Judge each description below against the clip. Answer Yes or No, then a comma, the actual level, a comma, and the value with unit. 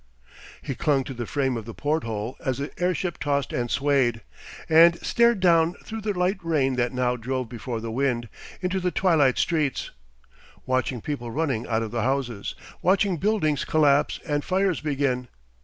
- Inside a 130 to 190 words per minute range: Yes, average, 170 wpm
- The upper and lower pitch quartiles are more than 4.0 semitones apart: Yes, wide, 5.4 semitones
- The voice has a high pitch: No, medium, 140 Hz